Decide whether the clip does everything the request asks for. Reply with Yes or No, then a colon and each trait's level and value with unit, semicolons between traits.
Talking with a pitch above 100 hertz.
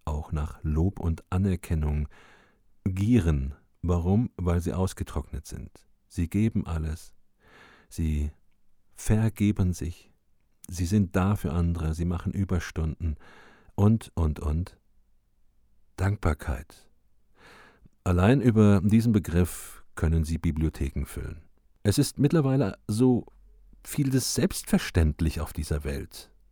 No: very low, 90 Hz